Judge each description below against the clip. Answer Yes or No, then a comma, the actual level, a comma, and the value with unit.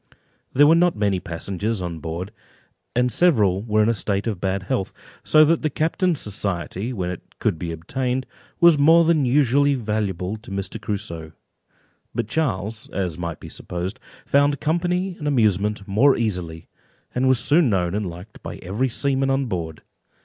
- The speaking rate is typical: Yes, average, 170 wpm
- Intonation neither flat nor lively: No, wide, 6.9 semitones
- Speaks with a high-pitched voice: No, low, 110 Hz